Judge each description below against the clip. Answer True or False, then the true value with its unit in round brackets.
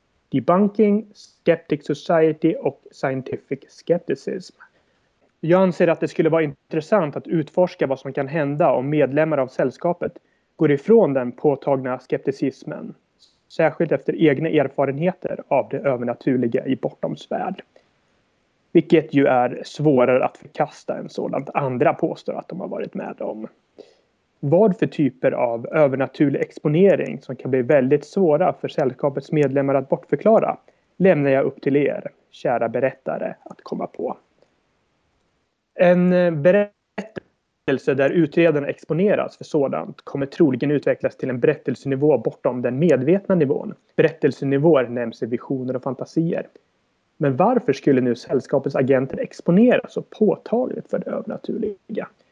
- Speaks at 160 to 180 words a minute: False (130 wpm)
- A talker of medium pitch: True (150 Hz)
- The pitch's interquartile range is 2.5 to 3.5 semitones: False (4.3 semitones)